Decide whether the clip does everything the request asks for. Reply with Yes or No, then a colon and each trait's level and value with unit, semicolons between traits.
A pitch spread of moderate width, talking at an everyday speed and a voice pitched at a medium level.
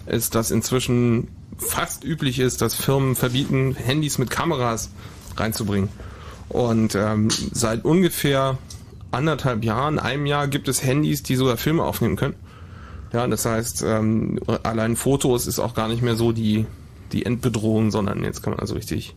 No: average, 3.5 semitones; average, 155 wpm; low, 115 Hz